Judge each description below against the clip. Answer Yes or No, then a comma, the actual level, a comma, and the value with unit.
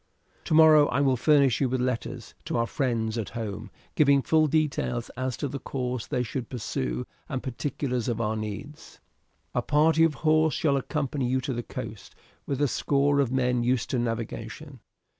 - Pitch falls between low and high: No, low, 130 Hz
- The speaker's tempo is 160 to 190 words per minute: Yes, average, 180 wpm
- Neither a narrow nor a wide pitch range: Yes, average, 3.4 semitones